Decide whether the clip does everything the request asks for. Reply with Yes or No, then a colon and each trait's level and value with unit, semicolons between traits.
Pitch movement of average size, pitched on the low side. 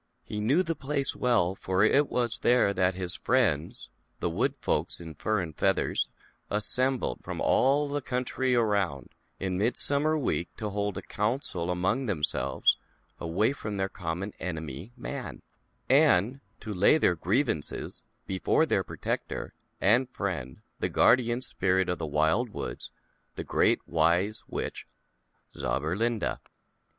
No: wide, 5.9 semitones; low, 105 Hz